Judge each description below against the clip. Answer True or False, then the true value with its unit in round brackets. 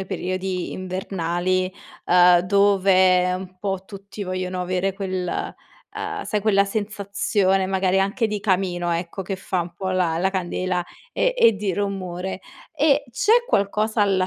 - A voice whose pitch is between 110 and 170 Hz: False (190 Hz)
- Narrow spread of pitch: True (1.6 semitones)